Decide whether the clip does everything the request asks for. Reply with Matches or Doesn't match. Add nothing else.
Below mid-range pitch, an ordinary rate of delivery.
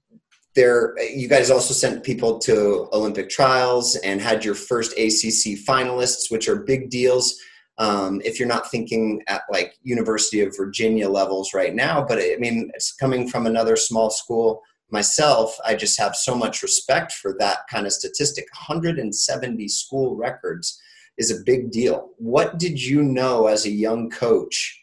Matches